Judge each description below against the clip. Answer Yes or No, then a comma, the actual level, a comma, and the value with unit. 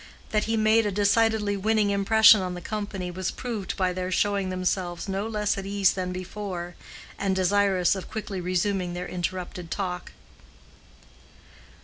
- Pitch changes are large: No, narrow, 2.4 semitones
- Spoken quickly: No, average, 150 wpm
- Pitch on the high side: Yes, high, 195 Hz